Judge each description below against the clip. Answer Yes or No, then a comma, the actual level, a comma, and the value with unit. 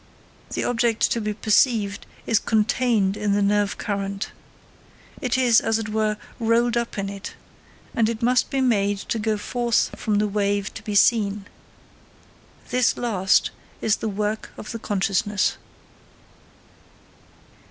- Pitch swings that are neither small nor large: No, narrow, 2.3 semitones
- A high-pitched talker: Yes, high, 215 Hz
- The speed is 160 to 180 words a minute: No, average, 140 wpm